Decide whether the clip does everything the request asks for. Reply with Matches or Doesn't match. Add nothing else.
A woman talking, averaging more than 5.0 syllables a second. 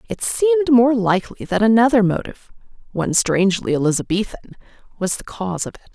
Matches